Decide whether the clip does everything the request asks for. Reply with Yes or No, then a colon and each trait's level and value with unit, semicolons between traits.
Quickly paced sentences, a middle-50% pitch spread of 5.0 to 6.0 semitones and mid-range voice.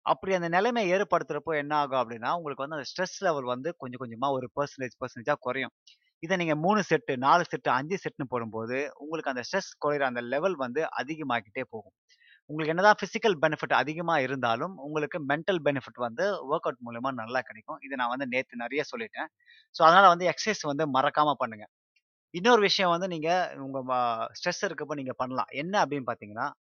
Yes: fast, 175 wpm; wide, 5.4 semitones; medium, 150 Hz